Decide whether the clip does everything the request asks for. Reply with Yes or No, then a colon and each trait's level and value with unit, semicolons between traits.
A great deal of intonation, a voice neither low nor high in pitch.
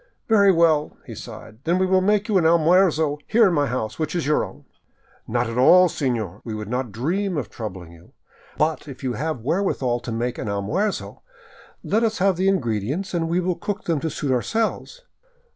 Yes: wide, 7.5 semitones; medium, 155 Hz